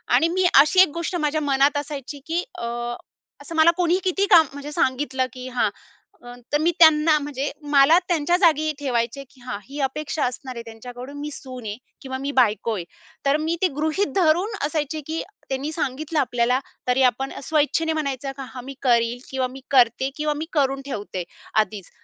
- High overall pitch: Yes, very high, 280 Hz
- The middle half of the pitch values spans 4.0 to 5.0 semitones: No, average, 3.6 semitones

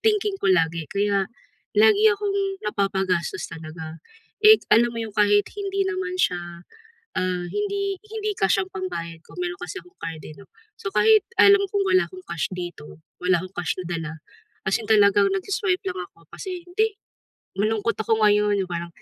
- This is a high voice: Yes, high, 215 Hz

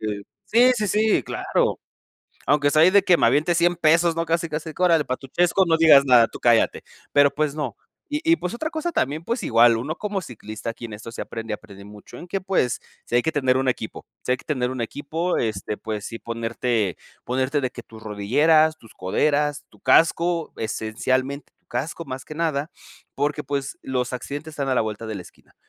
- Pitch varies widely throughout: Yes, wide, 6.0 semitones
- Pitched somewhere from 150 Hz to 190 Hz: No, medium, 140 Hz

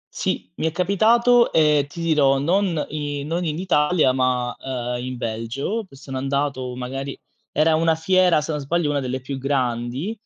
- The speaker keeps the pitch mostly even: No, average, 4.2 semitones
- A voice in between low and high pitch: Yes, medium, 145 Hz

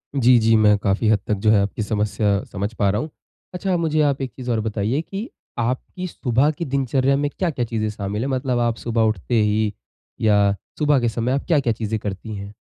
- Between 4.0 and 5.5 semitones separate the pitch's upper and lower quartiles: Yes, average, 4.5 semitones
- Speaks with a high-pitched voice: No, low, 115 Hz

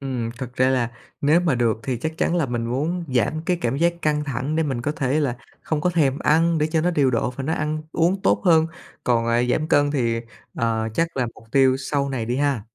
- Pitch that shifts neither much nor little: Yes, average, 4.4 semitones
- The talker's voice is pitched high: No, medium, 140 Hz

